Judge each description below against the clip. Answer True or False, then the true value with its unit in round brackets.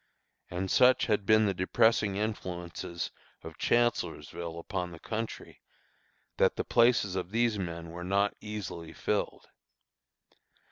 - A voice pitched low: True (95 Hz)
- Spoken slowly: True (130 wpm)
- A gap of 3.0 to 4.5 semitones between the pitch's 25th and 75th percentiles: True (3.9 semitones)